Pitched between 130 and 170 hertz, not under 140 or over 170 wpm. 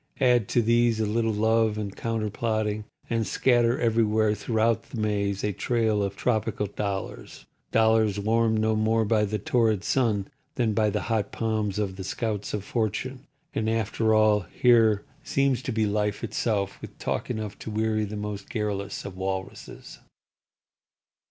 No: low, 110 Hz; average, 150 wpm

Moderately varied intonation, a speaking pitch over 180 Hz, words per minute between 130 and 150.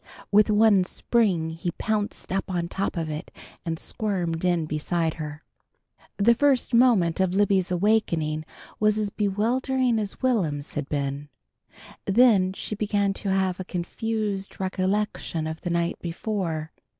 Yes: average, 4.3 semitones; high, 190 Hz; average, 140 wpm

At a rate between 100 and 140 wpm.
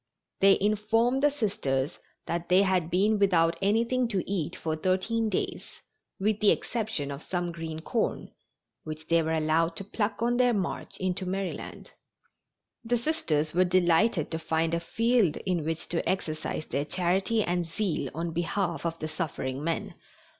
No: average, 160 wpm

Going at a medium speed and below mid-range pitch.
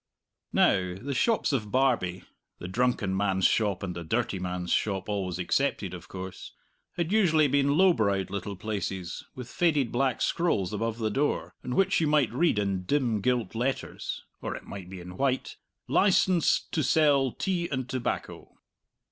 Yes: average, 165 wpm; low, 115 Hz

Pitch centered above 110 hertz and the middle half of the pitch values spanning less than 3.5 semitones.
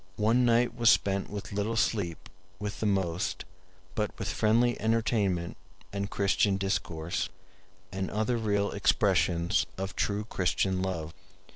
No: low, 100 Hz; average, 2.7 semitones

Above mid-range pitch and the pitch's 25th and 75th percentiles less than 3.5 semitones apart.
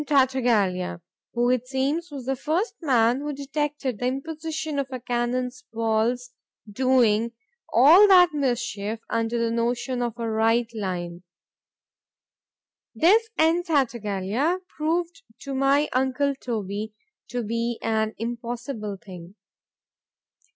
No: high, 245 Hz; average, 4.0 semitones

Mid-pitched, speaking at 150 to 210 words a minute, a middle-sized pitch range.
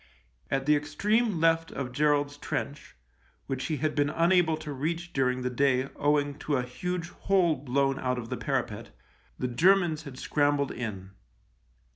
Yes: medium, 145 Hz; average, 160 wpm; average, 3.8 semitones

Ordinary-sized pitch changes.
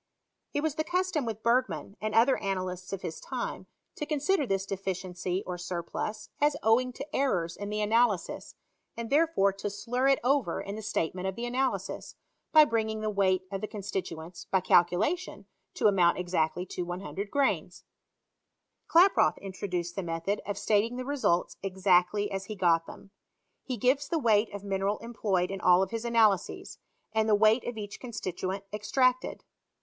Yes: average, 4.7 semitones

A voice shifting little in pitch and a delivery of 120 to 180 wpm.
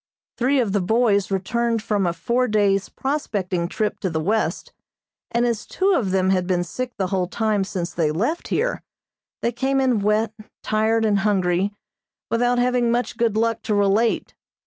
No: average, 3.7 semitones; average, 175 wpm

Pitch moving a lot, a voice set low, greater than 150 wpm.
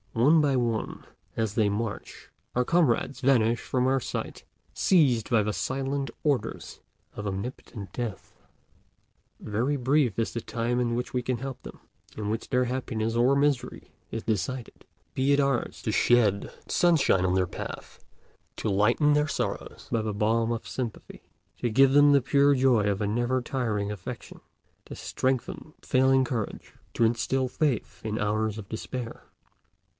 No: average, 3.4 semitones; low, 120 Hz; average, 160 wpm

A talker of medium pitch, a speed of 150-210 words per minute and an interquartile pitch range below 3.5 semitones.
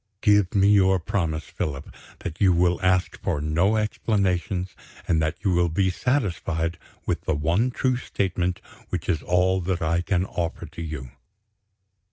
No: very low, 90 Hz; average, 160 wpm; average, 2.9 semitones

